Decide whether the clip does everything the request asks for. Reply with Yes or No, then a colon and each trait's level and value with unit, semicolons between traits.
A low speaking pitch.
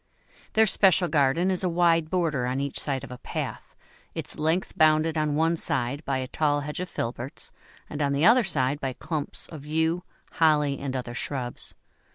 No: medium, 150 Hz